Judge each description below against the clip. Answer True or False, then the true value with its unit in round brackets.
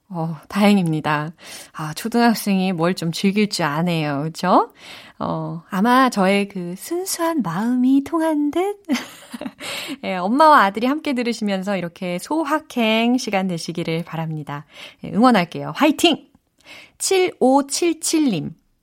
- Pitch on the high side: True (215 Hz)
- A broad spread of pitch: True (8.2 semitones)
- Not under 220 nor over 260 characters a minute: True (250 characters per minute)